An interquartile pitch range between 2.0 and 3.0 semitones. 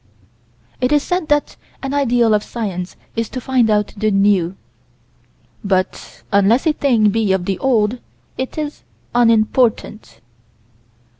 No: average, 4.3 semitones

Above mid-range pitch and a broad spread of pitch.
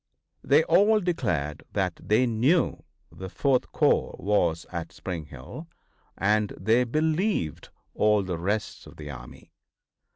No: low, 105 Hz; wide, 8.4 semitones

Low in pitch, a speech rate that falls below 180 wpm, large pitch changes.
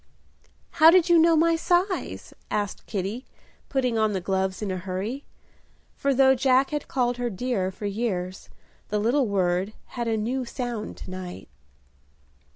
No: high, 235 Hz; average, 160 wpm; wide, 5.7 semitones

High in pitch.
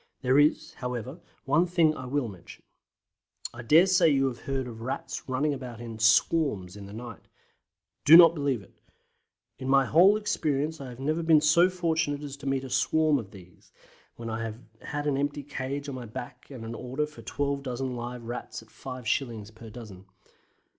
No: low, 135 Hz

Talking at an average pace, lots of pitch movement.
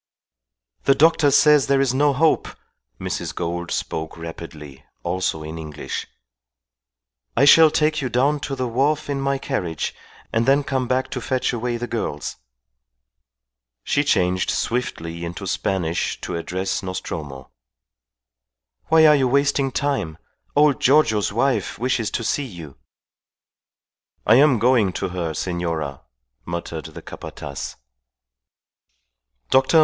No: slow, 130 wpm; wide, 8.2 semitones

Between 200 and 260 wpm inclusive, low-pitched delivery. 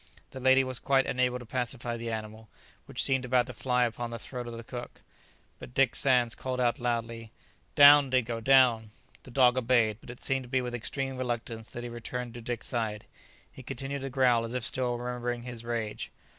Yes: fast, 205 wpm; low, 120 Hz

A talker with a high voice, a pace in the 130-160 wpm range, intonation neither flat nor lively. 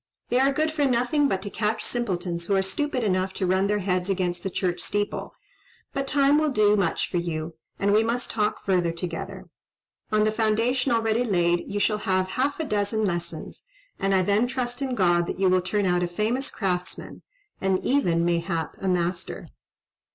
No: high, 200 Hz; average, 195 wpm; average, 4.9 semitones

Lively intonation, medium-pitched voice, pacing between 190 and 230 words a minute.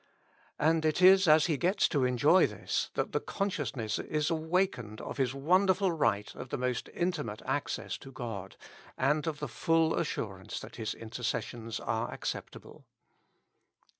No: wide, 6.2 semitones; medium, 150 Hz; average, 155 wpm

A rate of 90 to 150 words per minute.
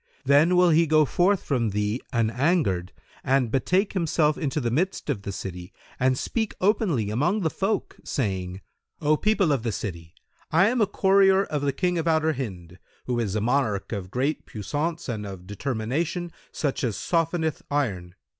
No: average, 175 wpm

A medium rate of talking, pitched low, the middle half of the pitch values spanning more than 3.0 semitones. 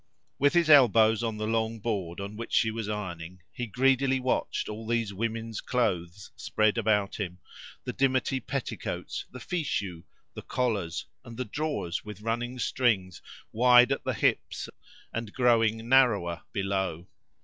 Yes: average, 150 wpm; low, 115 Hz; average, 3.8 semitones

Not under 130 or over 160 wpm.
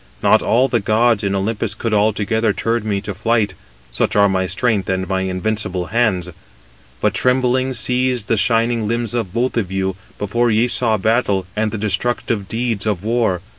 No: average, 175 wpm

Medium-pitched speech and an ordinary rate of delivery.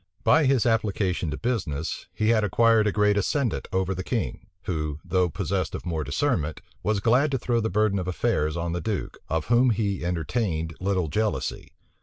No: low, 100 Hz; average, 185 wpm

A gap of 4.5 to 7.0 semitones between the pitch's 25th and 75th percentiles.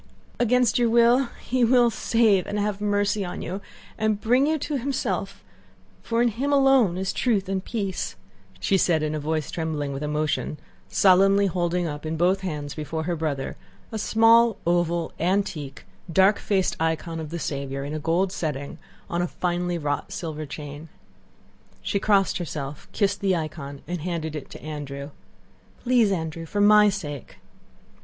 Yes: average, 5.1 semitones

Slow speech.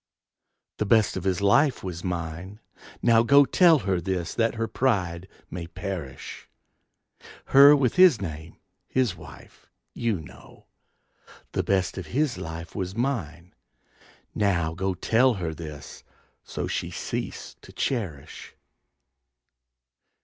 Yes: slow, 125 wpm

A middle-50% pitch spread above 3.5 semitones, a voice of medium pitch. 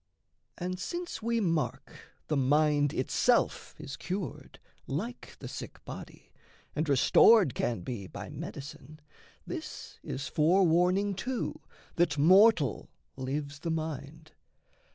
Yes: average, 4.6 semitones; medium, 155 Hz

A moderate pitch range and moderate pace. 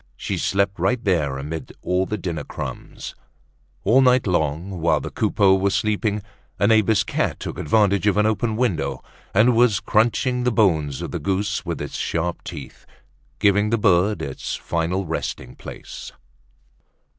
Yes: average, 4.3 semitones; average, 155 wpm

